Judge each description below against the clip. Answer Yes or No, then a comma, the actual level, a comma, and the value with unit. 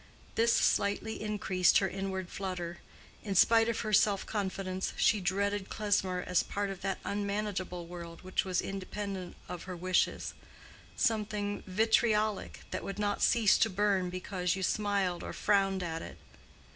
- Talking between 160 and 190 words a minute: No, average, 145 wpm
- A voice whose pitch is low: No, high, 195 Hz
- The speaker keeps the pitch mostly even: Yes, narrow, 2.1 semitones